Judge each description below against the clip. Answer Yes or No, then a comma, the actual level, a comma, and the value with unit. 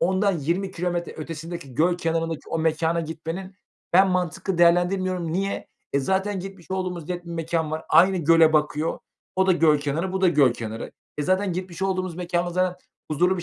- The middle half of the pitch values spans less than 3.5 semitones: Yes, narrow, 2.4 semitones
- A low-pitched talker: No, medium, 175 Hz